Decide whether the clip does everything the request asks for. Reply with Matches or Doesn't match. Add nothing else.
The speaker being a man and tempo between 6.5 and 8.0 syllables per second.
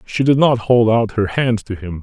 Doesn't match